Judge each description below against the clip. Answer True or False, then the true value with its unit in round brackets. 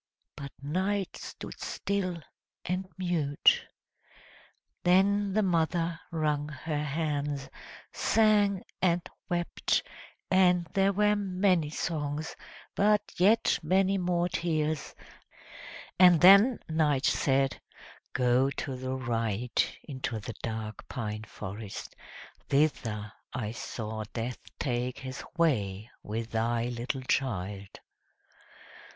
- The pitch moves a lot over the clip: True (6.9 semitones)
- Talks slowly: True (100 wpm)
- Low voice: False (150 Hz)